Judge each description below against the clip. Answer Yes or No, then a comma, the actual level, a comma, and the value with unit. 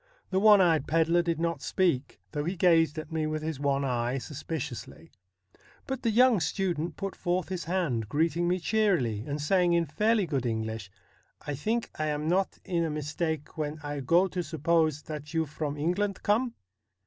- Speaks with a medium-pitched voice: Yes, medium, 160 Hz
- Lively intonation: No, average, 3.7 semitones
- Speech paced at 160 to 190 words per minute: Yes, average, 185 wpm